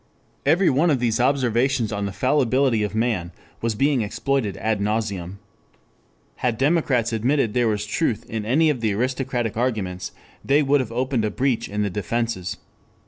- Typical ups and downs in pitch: Yes, average, 4.1 semitones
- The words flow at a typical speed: Yes, average, 165 wpm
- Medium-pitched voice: No, low, 115 Hz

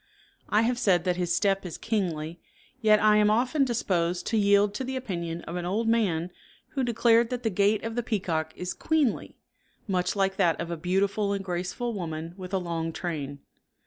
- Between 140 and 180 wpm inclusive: No, average, 195 wpm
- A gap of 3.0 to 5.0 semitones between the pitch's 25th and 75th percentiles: Yes, average, 4.3 semitones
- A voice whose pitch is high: Yes, high, 195 Hz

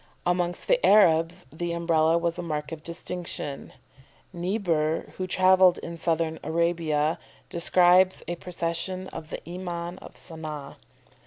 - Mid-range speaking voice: Yes, medium, 170 Hz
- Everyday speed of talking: No, slow, 130 wpm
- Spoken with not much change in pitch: Yes, narrow, 1.8 semitones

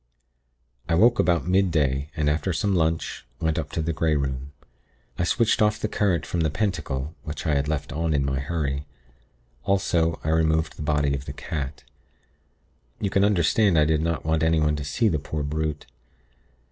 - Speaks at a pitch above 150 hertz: No, very low, 80 Hz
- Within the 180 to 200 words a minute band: Yes, average, 185 wpm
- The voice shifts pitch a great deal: No, average, 2.8 semitones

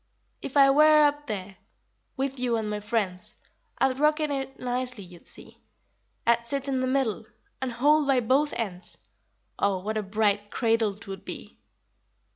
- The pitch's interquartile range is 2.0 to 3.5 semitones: No, average, 4.7 semitones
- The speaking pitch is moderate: No, high, 245 Hz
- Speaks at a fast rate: No, average, 165 wpm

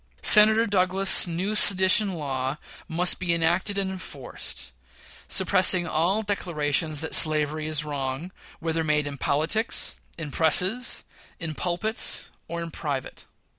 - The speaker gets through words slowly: Yes, slow, 125 wpm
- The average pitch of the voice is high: No, medium, 170 Hz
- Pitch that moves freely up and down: No, average, 3.8 semitones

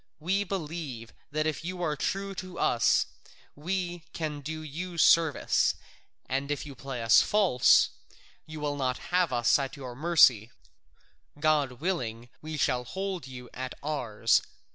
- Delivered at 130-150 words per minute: Yes, average, 145 wpm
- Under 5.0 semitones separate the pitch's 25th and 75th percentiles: No, average, 5.3 semitones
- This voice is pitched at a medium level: Yes, medium, 150 Hz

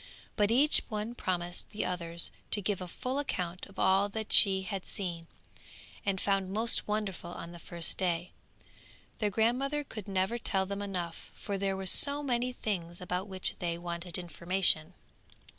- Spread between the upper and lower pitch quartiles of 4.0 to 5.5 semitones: No, average, 3.3 semitones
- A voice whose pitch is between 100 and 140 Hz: No, high, 190 Hz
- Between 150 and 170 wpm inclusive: Yes, average, 165 wpm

